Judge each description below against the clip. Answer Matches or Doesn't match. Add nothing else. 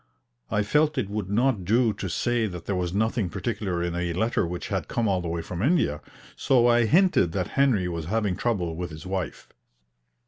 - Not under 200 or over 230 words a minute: Matches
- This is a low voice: Matches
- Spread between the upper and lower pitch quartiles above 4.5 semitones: Matches